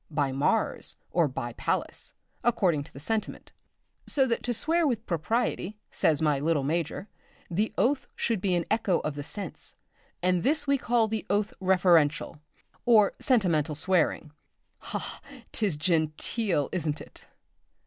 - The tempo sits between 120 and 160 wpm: Yes, average, 150 wpm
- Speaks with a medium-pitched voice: Yes, medium, 180 Hz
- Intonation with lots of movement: Yes, wide, 6.4 semitones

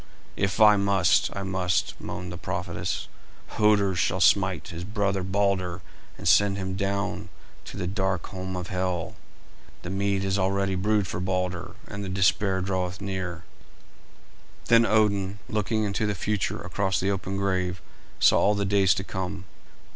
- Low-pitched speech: Yes, very low, 95 Hz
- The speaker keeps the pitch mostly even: Yes, narrow, 1.4 semitones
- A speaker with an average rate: Yes, average, 155 wpm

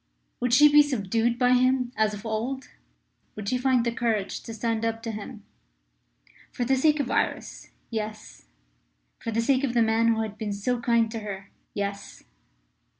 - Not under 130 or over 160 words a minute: No, average, 180 wpm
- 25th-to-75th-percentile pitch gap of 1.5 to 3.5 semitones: Yes, narrow, 2.6 semitones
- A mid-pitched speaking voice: No, high, 230 Hz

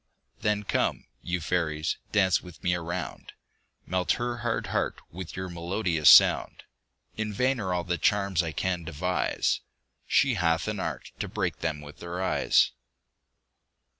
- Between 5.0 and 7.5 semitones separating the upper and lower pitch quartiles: No, average, 2.9 semitones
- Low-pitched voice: Yes, very low, 90 Hz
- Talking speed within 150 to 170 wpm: Yes, average, 155 wpm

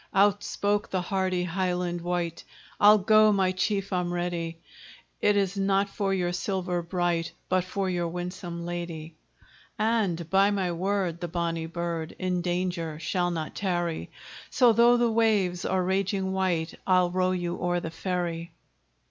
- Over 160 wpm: No, average, 155 wpm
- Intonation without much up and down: Yes, narrow, 2.1 semitones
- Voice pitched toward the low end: No, medium, 180 Hz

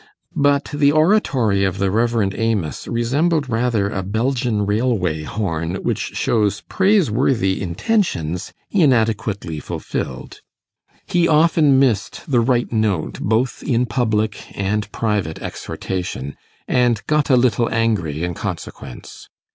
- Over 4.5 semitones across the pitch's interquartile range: Yes, average, 5.1 semitones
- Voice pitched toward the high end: No, low, 115 Hz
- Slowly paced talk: Yes, slow, 115 wpm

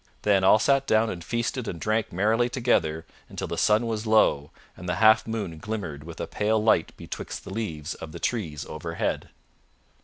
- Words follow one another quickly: No, average, 185 wpm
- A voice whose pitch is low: Yes, low, 105 Hz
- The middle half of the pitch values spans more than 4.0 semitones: Yes, average, 5.0 semitones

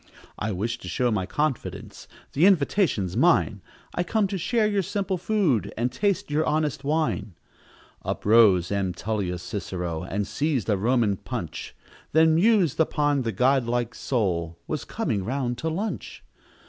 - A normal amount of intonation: No, wide, 7.8 semitones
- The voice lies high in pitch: No, low, 125 Hz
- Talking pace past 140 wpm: Yes, average, 155 wpm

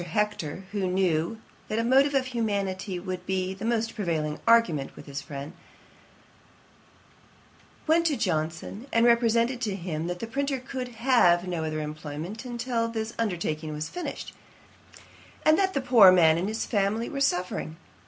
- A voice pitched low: No, high, 200 Hz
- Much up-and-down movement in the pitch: Yes, wide, 5.7 semitones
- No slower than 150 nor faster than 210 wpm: Yes, average, 155 wpm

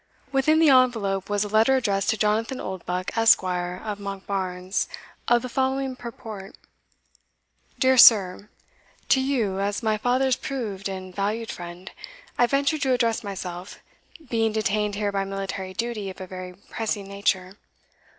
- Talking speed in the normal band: Yes, average, 145 wpm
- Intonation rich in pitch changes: No, average, 3.8 semitones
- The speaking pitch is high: Yes, high, 210 Hz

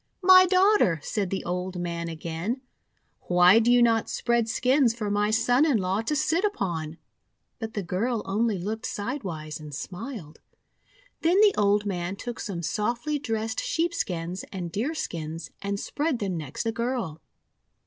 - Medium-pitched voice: No, high, 210 Hz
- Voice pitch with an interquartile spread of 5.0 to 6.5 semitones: Yes, wide, 5.6 semitones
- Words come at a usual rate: Yes, average, 155 wpm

